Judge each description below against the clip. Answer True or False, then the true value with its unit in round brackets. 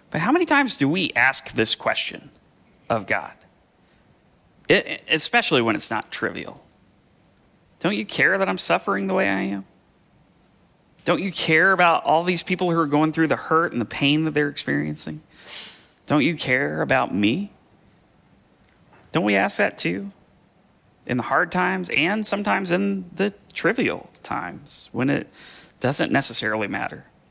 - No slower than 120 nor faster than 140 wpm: False (155 wpm)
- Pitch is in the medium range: True (160 Hz)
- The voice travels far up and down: True (7.7 semitones)